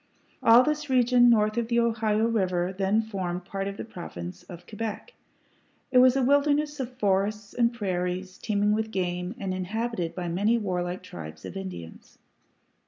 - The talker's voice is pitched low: No, high, 210 Hz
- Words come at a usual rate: Yes, average, 165 wpm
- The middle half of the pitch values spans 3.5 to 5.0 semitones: Yes, average, 4.3 semitones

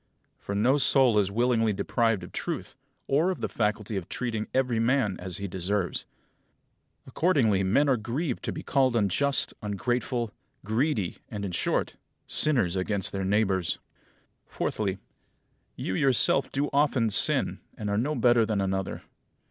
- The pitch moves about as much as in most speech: Yes, average, 4.6 semitones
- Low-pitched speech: Yes, low, 110 Hz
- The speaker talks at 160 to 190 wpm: No, average, 150 wpm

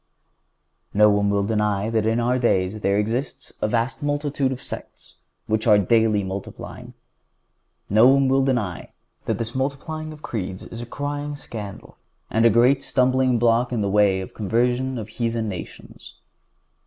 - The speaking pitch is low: Yes, low, 115 Hz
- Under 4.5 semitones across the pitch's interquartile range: Yes, average, 4.0 semitones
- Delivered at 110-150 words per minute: No, average, 165 wpm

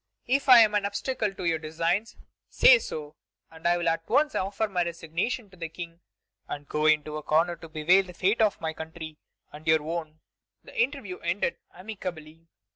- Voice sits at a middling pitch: Yes, medium, 170 Hz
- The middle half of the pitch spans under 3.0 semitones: No, average, 4.3 semitones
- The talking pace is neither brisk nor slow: Yes, average, 190 wpm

